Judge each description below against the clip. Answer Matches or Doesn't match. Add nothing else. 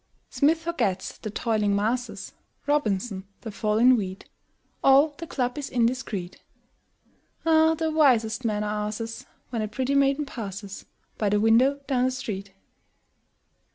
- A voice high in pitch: Matches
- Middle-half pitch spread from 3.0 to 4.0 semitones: Doesn't match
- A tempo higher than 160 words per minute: Doesn't match